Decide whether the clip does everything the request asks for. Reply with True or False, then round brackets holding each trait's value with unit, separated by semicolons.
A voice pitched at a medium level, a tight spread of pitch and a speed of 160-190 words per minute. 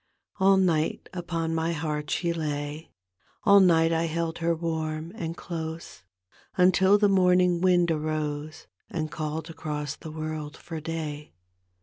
False (165 Hz; 1.9 semitones; 135 wpm)